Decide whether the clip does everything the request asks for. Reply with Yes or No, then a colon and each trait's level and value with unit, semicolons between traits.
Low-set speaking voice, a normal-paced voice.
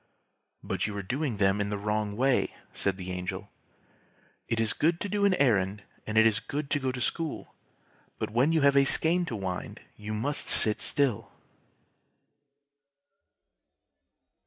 Yes: low, 115 Hz; average, 160 wpm